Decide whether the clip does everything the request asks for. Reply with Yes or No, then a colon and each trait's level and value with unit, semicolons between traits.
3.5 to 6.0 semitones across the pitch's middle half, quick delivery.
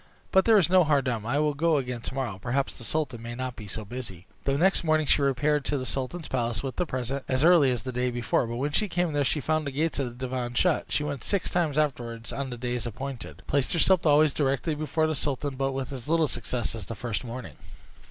Yes: average, 3.9 semitones; fast, 250 wpm